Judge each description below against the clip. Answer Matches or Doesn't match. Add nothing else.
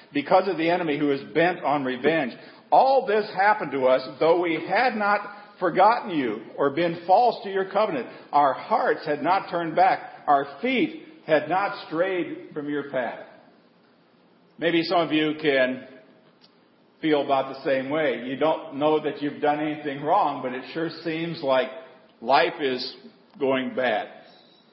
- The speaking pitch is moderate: Matches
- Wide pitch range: Matches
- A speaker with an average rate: Matches